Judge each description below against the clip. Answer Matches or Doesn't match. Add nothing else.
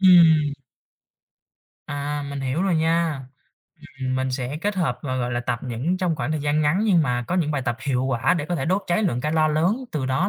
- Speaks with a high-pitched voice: Doesn't match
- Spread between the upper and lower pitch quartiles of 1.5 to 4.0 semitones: Doesn't match